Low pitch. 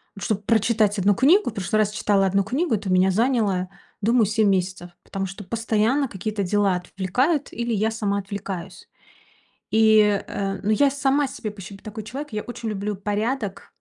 No: high, 210 Hz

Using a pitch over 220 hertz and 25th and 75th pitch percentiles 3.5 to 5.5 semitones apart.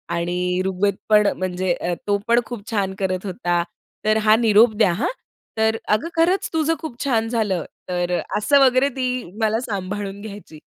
No: high, 210 Hz; average, 3.9 semitones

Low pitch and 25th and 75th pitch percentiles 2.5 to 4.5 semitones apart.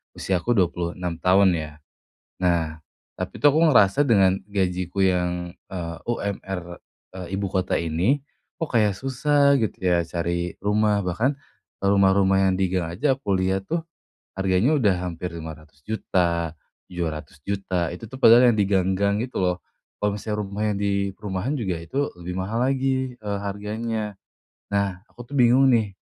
Yes: very low, 95 Hz; average, 3.6 semitones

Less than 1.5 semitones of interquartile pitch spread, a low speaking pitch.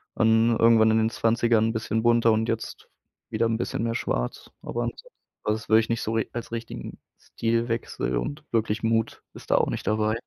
Yes: narrow, 0.9 semitones; low, 115 Hz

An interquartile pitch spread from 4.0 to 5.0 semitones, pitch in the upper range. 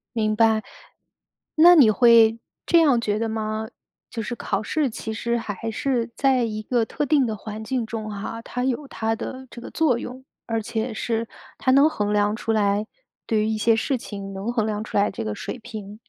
No: narrow, 2.4 semitones; high, 225 Hz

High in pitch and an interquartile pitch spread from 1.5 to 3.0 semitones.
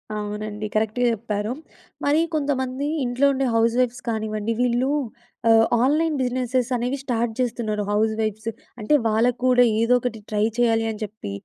Yes: high, 235 Hz; narrow, 2.6 semitones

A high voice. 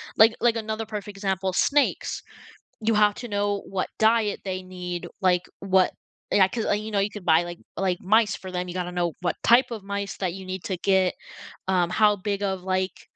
Yes: high, 195 Hz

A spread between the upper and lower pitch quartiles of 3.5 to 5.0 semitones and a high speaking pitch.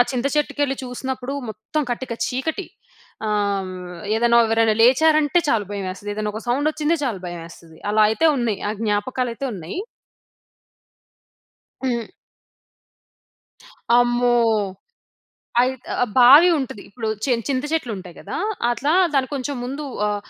Yes: average, 4.4 semitones; high, 245 Hz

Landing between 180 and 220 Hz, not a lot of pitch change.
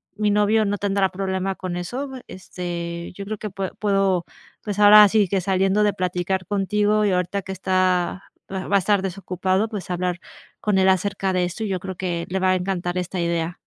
Yes: high, 190 Hz; narrow, 2.0 semitones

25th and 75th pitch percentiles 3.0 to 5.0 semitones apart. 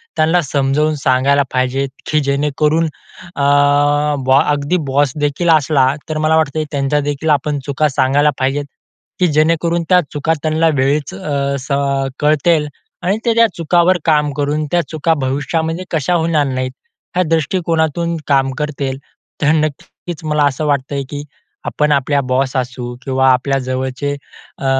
No: narrow, 2.6 semitones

